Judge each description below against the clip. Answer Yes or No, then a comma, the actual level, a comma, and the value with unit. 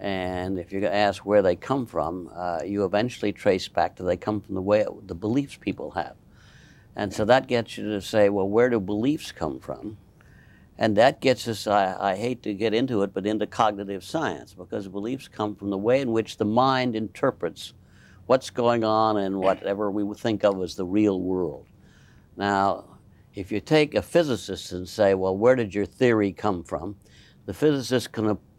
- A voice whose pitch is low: Yes, low, 105 Hz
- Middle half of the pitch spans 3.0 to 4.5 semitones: No, narrow, 2.5 semitones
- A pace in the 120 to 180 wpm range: No, average, 190 wpm